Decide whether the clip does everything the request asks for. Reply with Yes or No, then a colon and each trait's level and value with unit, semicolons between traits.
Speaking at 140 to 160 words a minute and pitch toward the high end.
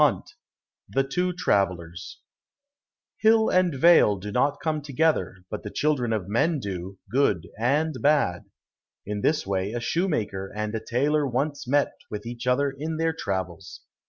No: average, 155 wpm; low, 125 Hz